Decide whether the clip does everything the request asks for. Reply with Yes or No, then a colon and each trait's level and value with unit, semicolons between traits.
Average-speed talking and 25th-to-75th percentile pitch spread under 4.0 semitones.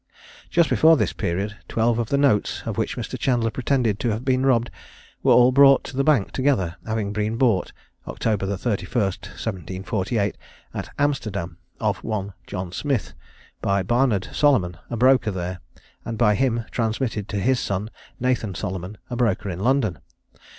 No: average, 160 wpm; average, 4.5 semitones